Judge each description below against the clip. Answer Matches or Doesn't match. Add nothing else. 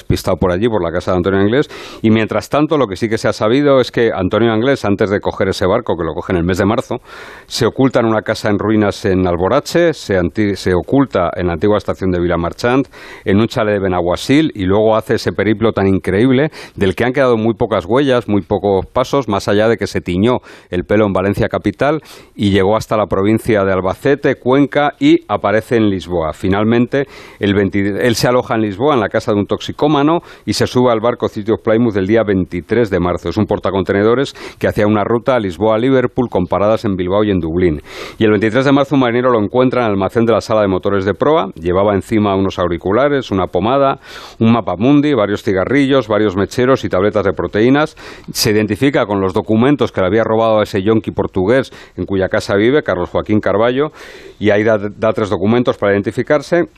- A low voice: Matches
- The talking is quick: Matches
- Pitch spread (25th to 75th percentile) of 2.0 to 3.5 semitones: Doesn't match